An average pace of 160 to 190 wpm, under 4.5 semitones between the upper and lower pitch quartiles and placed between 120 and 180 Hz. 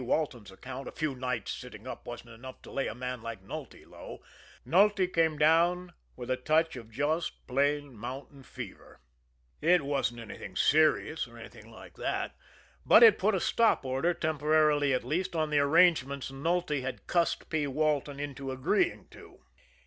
Yes: average, 165 wpm; average, 3.9 semitones; medium, 140 Hz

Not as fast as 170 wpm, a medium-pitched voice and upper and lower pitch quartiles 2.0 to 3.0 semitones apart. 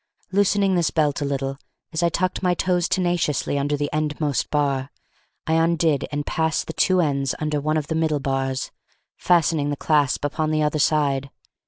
No: average, 180 wpm; medium, 155 Hz; narrow, 2.5 semitones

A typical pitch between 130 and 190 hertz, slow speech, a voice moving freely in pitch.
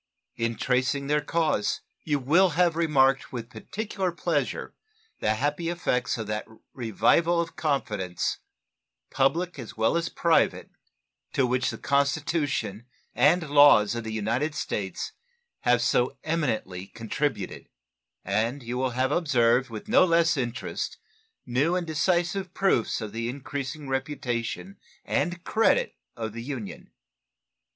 Yes: low, 135 Hz; slow, 130 wpm; wide, 6.0 semitones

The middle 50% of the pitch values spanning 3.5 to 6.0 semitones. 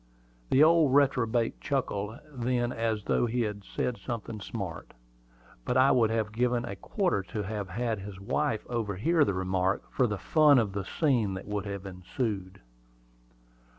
Yes: average, 4.0 semitones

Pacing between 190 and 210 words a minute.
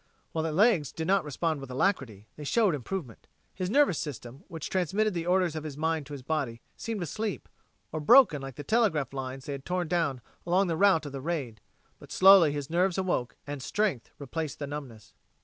Yes: average, 200 wpm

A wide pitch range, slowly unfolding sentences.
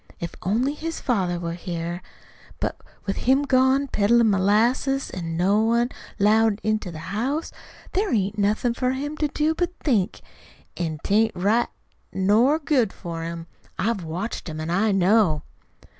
No: wide, 6.0 semitones; average, 160 wpm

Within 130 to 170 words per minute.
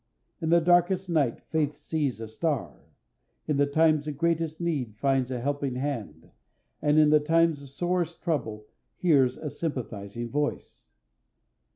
Yes: average, 150 wpm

